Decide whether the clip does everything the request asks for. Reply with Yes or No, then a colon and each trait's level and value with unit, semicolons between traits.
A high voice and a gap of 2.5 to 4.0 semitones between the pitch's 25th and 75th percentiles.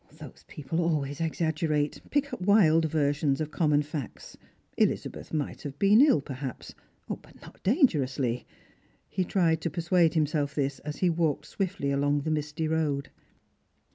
No: medium, 155 Hz; average, 2.8 semitones